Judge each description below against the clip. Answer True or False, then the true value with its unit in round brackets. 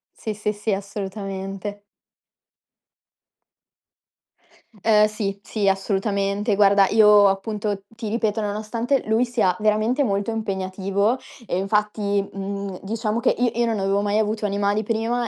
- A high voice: True (210 Hz)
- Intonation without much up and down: True (1.9 semitones)